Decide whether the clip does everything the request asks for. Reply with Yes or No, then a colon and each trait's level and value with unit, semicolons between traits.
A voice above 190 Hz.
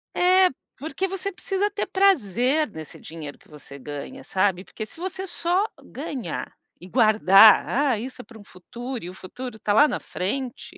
Yes: high, 245 Hz